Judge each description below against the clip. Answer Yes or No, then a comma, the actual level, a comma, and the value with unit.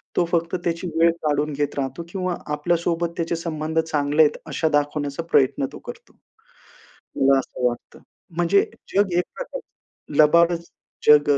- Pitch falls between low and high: Yes, medium, 160 Hz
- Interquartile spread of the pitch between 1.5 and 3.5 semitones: Yes, average, 2.7 semitones